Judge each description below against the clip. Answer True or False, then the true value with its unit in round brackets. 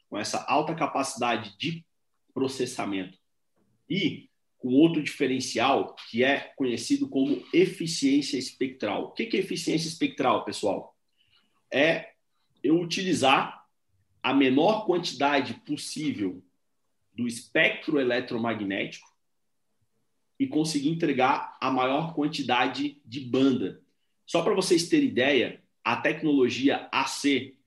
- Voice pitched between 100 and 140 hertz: True (135 Hz)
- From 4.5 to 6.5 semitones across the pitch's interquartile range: True (5.1 semitones)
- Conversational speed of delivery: False (105 wpm)